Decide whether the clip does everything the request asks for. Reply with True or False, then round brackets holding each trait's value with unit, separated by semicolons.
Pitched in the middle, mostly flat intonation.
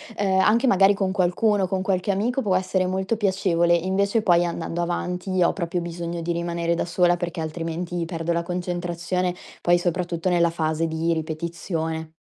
True (175 Hz; 1.9 semitones)